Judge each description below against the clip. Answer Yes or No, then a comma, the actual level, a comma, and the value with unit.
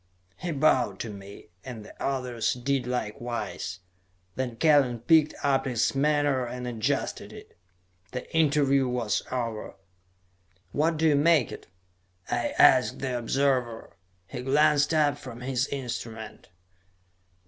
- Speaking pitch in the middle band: No, low, 130 Hz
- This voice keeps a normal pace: No, slow, 125 wpm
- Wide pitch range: No, average, 3.4 semitones